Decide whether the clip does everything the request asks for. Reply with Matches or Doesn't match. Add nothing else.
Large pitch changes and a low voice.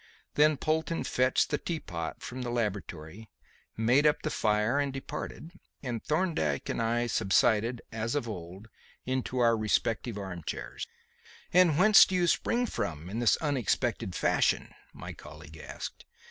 Matches